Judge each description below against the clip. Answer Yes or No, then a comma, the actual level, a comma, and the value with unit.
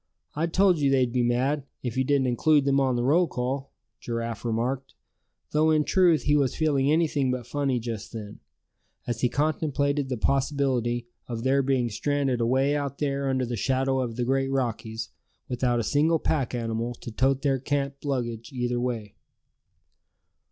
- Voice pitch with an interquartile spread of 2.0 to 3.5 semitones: Yes, average, 2.8 semitones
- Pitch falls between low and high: No, low, 130 Hz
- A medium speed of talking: Yes, average, 175 wpm